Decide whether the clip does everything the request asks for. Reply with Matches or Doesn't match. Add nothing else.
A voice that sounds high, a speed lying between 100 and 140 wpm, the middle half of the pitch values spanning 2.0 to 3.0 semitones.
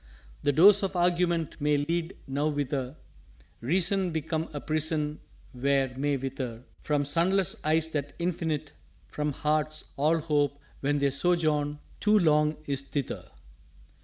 Doesn't match